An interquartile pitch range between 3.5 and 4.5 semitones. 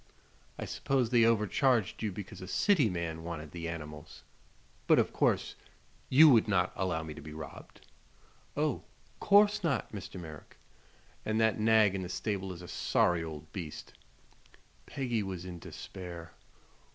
No: average, 5.0 semitones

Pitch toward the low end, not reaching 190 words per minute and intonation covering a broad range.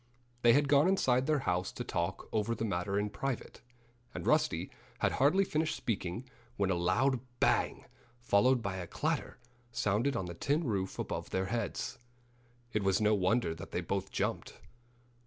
Yes: low, 110 Hz; average, 170 wpm; wide, 5.8 semitones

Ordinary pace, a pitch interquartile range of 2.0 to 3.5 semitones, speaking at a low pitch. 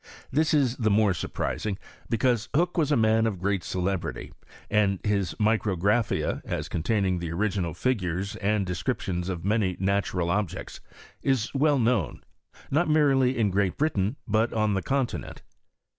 No: average, 145 wpm; average, 4.6 semitones; low, 105 Hz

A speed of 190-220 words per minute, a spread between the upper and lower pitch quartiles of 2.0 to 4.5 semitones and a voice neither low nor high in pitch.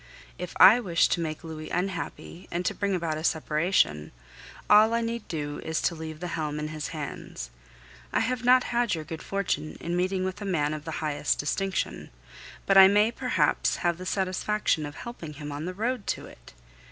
Yes: average, 200 wpm; average, 4.2 semitones; medium, 175 Hz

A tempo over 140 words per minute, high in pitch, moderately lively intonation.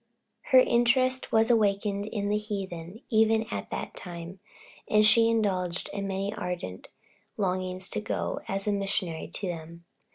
Yes: average, 150 wpm; high, 200 Hz; average, 3.2 semitones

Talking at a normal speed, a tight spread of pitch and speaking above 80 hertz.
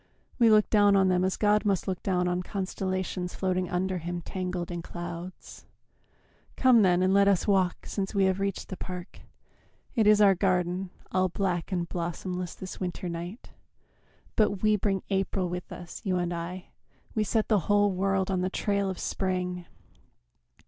Yes: average, 175 wpm; narrow, 1.8 semitones; medium, 185 Hz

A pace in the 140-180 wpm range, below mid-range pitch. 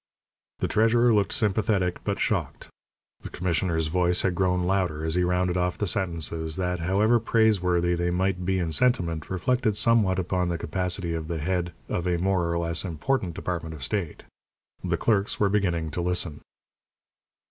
Yes: average, 170 wpm; very low, 90 Hz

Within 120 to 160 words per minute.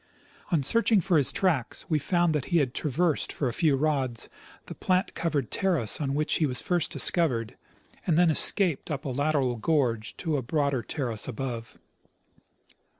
No: average, 170 wpm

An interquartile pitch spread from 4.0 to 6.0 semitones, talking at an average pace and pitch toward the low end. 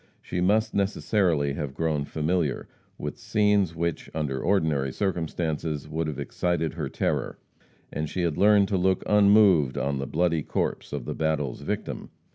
Yes: average, 4.4 semitones; average, 155 wpm; very low, 80 Hz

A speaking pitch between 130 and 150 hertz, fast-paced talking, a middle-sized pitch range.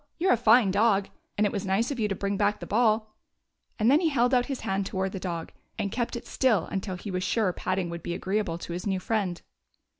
No: high, 205 Hz; fast, 260 wpm; average, 3.4 semitones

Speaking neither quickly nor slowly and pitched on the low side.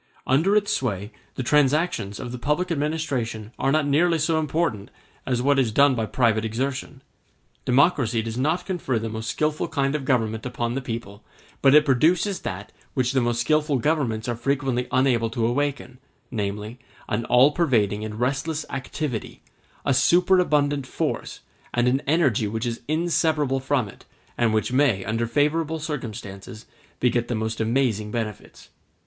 Yes: average, 160 wpm; low, 130 Hz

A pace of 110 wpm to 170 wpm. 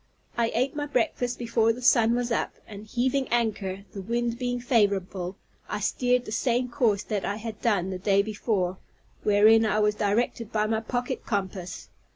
No: average, 180 wpm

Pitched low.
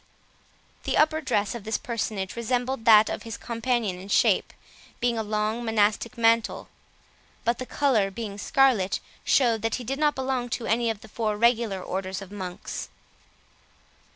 No: high, 225 Hz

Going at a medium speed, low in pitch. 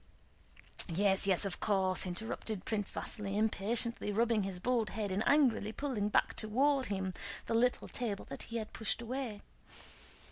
No: average, 150 wpm; high, 215 Hz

